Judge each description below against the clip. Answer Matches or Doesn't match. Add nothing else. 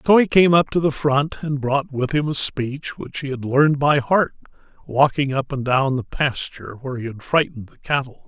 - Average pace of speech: Doesn't match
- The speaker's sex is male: Matches